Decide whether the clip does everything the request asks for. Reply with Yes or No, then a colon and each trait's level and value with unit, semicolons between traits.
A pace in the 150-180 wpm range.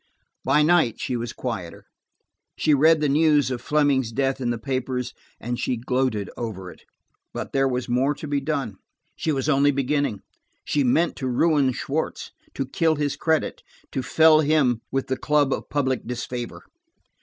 Yes: average, 170 wpm